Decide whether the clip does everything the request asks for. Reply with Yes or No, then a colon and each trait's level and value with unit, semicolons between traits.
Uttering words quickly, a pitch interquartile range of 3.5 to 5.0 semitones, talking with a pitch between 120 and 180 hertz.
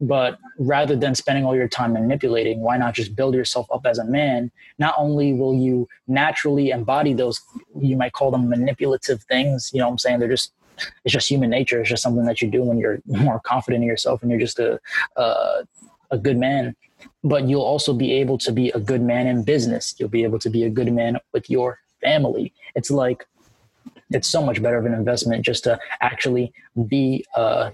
No: fast, 215 wpm; narrow, 2.4 semitones; low, 125 Hz